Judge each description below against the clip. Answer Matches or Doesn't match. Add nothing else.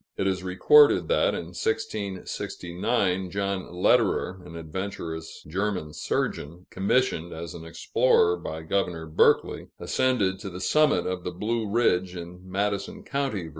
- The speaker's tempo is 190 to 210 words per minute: Doesn't match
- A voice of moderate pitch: Doesn't match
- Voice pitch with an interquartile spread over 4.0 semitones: Doesn't match